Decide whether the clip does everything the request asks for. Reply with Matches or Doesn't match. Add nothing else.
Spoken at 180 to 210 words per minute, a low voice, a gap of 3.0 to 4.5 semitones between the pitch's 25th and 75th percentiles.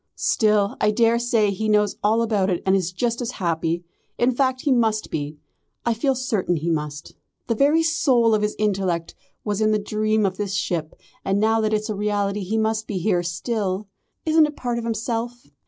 Doesn't match